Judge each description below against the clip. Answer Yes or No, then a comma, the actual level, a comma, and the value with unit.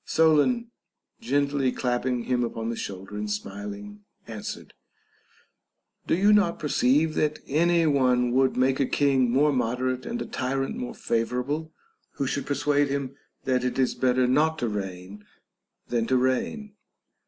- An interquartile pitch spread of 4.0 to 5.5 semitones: No, average, 3.2 semitones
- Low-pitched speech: Yes, low, 130 Hz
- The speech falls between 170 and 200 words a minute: No, average, 150 wpm